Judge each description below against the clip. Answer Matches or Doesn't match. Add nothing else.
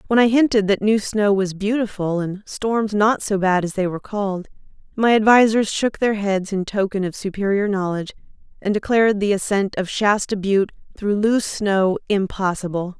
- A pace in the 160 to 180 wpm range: Matches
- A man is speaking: Doesn't match